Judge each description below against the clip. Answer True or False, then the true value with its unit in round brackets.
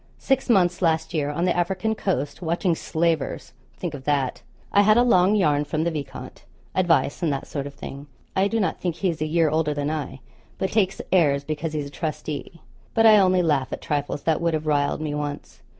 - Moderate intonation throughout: True (3.9 semitones)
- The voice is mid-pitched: True (160 Hz)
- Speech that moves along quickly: True (215 wpm)